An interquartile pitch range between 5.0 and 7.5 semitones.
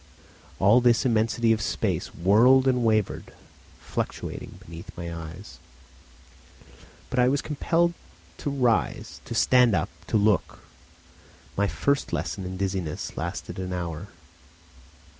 Yes: average, 5.3 semitones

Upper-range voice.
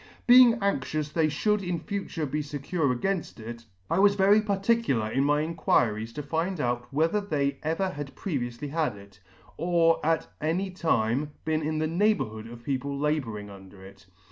No: medium, 150 Hz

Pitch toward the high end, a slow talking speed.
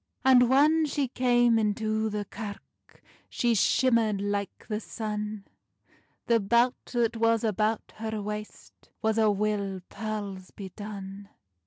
Yes: high, 215 Hz; slow, 125 wpm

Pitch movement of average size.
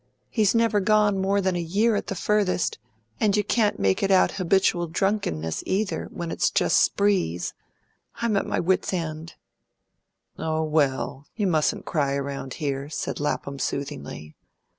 No: wide, 6.1 semitones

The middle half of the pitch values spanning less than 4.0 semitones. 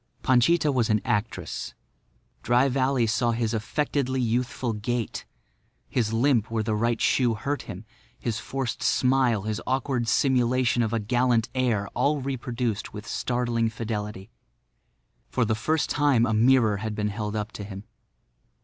Yes: average, 2.9 semitones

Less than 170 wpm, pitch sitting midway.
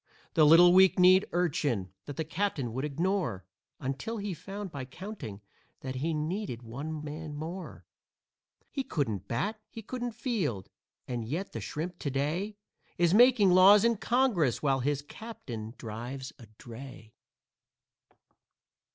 Yes: average, 140 wpm; medium, 155 Hz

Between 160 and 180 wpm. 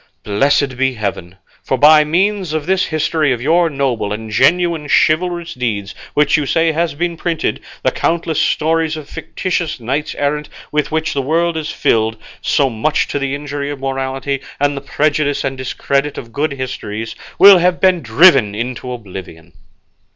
Yes: average, 165 wpm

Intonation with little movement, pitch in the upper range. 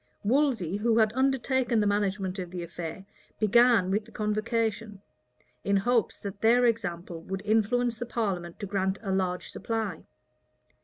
No: average, 3.3 semitones; high, 210 Hz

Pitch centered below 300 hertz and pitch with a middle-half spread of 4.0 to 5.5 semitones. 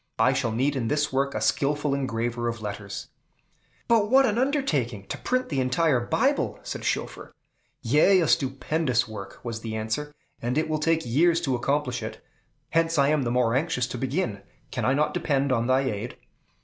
Yes: low, 135 Hz; average, 4.5 semitones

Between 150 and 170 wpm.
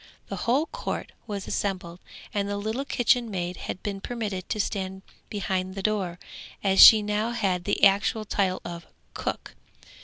Yes: average, 160 wpm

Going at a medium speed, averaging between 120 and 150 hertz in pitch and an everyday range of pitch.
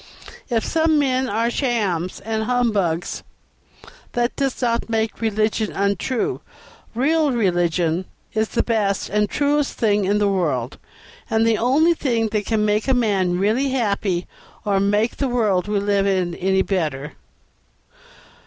No: average, 145 wpm; high, 215 Hz; average, 3.8 semitones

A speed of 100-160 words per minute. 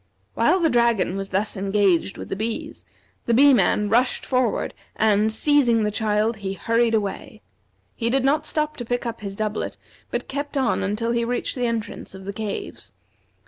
No: average, 185 wpm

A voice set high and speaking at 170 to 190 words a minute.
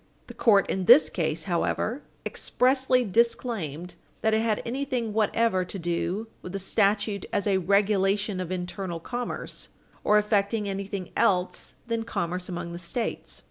No: high, 200 Hz; average, 145 wpm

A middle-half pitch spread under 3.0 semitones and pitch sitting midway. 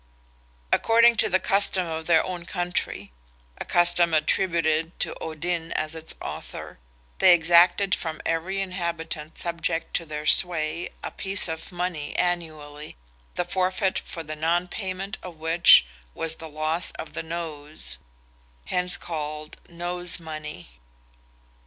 Yes: narrow, 2.4 semitones; medium, 165 Hz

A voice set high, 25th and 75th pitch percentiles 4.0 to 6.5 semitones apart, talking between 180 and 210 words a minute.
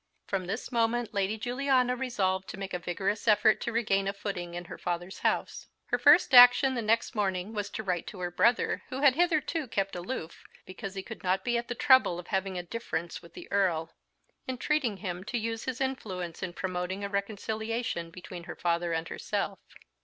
Yes: high, 200 Hz; average, 4.9 semitones; average, 200 wpm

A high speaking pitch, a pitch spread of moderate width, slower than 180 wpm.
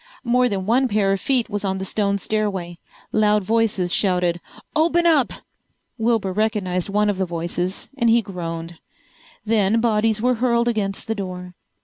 Yes: high, 210 Hz; average, 3.6 semitones; average, 160 wpm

